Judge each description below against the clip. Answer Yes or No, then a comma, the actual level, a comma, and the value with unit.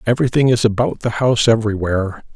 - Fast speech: No, average, 155 wpm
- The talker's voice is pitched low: Yes, low, 115 Hz